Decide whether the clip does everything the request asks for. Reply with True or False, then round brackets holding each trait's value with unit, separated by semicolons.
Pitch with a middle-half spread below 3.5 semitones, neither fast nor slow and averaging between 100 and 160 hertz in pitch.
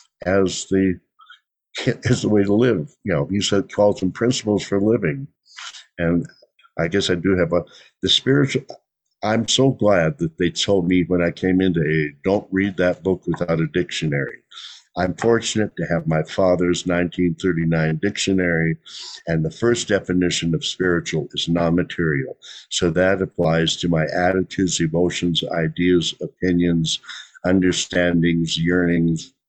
False (2.5 semitones; 150 wpm; 90 Hz)